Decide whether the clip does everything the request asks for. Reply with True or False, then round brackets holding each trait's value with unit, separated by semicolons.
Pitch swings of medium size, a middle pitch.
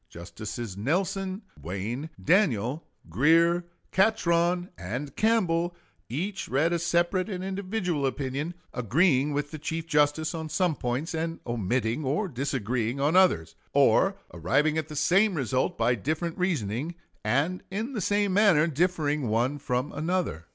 False (6.0 semitones; 155 Hz)